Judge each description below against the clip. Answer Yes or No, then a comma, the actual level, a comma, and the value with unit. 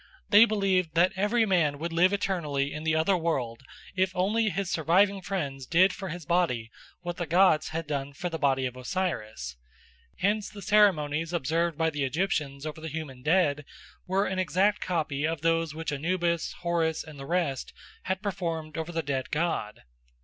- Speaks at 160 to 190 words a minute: Yes, average, 180 wpm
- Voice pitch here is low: No, medium, 165 Hz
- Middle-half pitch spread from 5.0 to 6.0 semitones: No, average, 4.0 semitones